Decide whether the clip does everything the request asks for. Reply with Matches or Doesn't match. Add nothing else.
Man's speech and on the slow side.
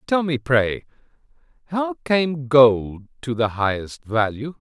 Matches